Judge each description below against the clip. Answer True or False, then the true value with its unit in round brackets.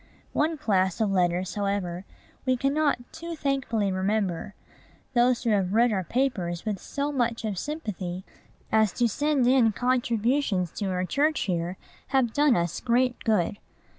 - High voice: True (225 Hz)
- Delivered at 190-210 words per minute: False (150 wpm)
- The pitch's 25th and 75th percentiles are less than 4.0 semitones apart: False (5.5 semitones)